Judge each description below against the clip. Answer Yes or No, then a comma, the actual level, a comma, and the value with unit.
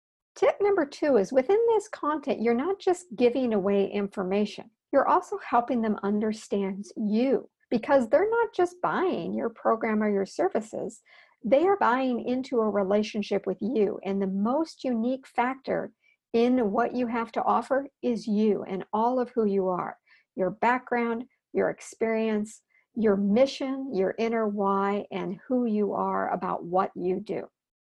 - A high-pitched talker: Yes, high, 230 Hz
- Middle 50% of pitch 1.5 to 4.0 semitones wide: No, average, 4.5 semitones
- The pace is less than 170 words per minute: Yes, average, 155 wpm